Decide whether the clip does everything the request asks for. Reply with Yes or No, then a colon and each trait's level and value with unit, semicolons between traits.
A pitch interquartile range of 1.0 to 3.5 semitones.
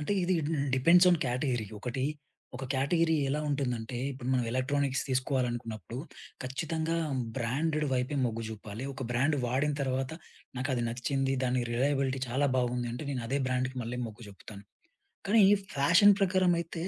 Yes: average, 3.1 semitones